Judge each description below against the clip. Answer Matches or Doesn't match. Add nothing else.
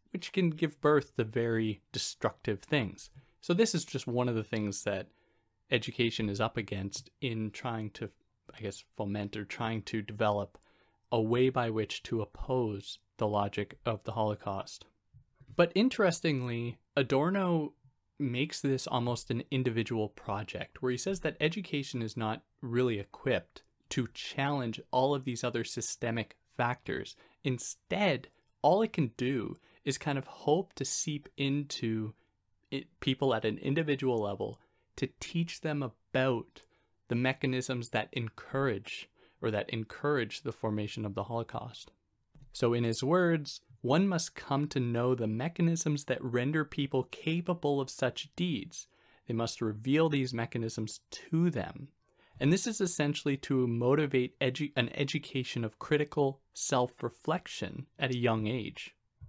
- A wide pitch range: Doesn't match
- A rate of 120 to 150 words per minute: Matches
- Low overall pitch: Matches